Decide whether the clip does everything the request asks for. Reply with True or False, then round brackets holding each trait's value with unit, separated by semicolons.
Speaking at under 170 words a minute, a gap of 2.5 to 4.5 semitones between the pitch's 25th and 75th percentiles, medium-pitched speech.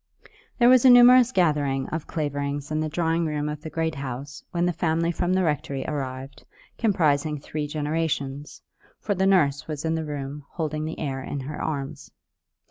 False (180 wpm; 2.8 semitones; 155 Hz)